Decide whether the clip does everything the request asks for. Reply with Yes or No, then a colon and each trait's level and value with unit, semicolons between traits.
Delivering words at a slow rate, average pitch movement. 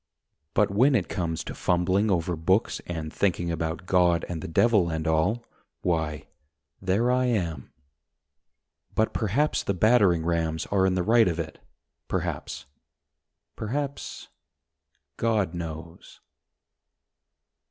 Yes: slow, 120 wpm; average, 4.7 semitones